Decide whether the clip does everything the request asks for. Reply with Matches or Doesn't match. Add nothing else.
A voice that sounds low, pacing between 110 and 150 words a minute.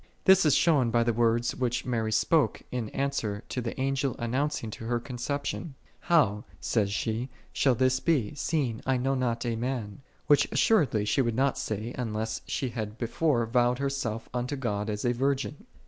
Doesn't match